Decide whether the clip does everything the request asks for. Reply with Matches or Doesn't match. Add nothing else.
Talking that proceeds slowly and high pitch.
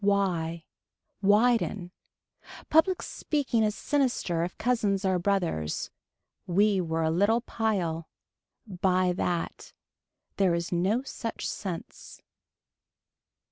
Matches